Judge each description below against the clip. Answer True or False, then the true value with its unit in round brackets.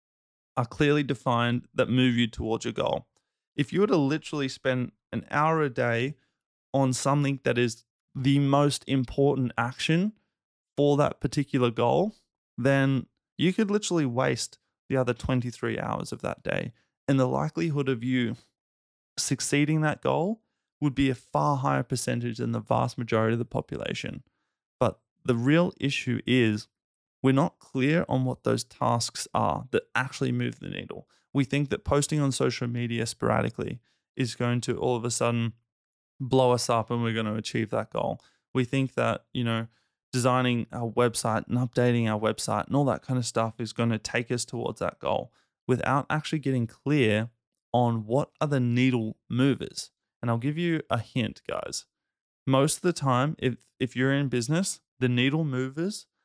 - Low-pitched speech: True (130 Hz)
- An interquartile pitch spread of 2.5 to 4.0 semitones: True (3.0 semitones)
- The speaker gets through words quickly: False (175 wpm)